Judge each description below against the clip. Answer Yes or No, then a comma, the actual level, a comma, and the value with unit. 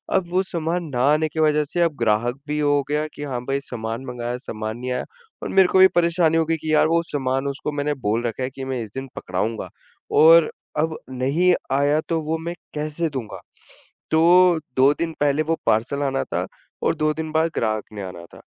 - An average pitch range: Yes, average, 4.2 semitones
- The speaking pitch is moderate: Yes, medium, 150 Hz